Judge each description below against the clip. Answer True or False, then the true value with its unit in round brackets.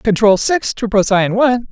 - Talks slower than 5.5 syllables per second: True (4.8 syllables/s)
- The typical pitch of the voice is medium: False (220 Hz)